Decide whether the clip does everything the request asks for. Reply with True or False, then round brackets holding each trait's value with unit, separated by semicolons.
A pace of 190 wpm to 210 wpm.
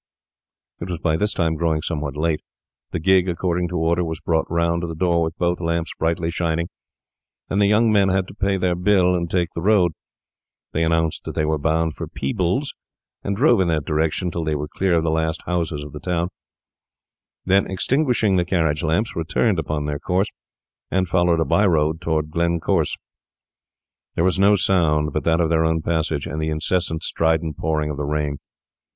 True (195 wpm)